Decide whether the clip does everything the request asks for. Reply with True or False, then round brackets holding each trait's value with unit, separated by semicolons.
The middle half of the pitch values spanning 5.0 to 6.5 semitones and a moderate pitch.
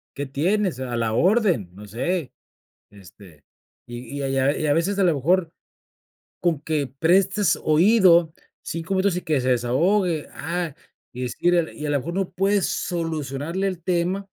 True (5.4 semitones; 165 Hz)